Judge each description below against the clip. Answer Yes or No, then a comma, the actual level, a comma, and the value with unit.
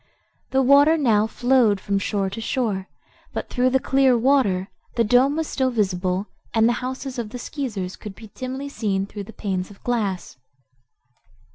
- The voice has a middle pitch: No, high, 230 Hz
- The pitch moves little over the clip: No, average, 4.7 semitones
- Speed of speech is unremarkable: Yes, average, 170 wpm